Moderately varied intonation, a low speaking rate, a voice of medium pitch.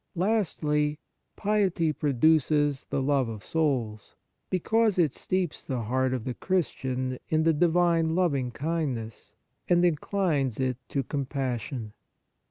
Yes: average, 4.8 semitones; slow, 125 wpm; medium, 150 Hz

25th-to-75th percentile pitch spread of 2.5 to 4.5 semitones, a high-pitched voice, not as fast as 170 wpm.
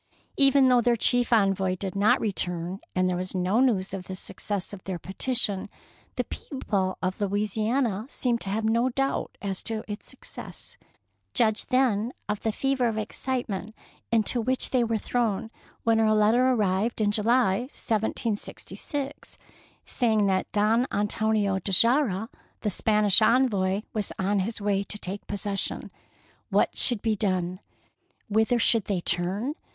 Yes: average, 3.3 semitones; high, 215 Hz; average, 150 wpm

